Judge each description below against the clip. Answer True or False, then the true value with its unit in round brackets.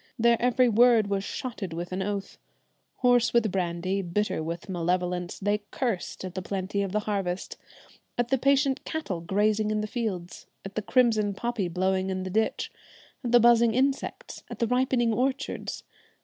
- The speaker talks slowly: False (170 wpm)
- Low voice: False (210 Hz)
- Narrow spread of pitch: False (4.2 semitones)